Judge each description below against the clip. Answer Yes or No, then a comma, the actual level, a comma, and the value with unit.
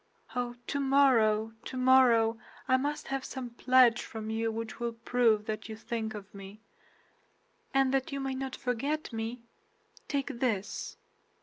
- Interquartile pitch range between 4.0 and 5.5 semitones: No, average, 3.0 semitones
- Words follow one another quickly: No, average, 140 wpm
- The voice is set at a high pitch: Yes, high, 240 Hz